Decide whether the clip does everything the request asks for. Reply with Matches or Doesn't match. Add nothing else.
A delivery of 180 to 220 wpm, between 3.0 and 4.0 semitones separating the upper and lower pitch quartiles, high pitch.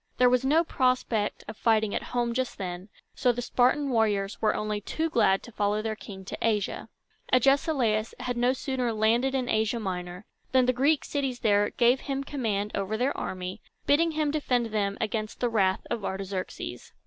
Matches